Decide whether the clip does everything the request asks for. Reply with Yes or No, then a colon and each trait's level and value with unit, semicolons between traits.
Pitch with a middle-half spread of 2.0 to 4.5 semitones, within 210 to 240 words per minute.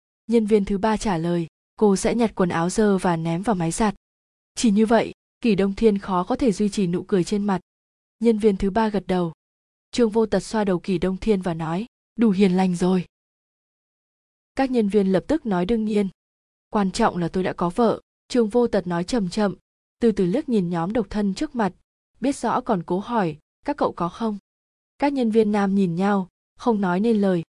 Yes: average, 3.6 semitones; average, 220 wpm